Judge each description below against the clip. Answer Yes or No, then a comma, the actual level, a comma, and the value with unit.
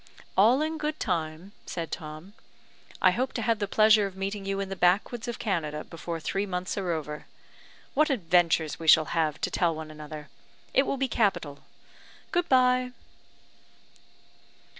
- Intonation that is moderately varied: No, wide, 6.1 semitones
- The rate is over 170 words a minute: No, average, 160 wpm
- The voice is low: No, high, 190 Hz